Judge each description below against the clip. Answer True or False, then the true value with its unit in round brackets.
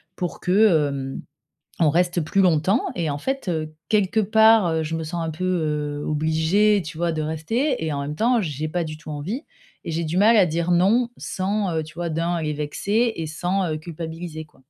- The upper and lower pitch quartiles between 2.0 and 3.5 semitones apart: False (4.0 semitones)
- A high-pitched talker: False (165 Hz)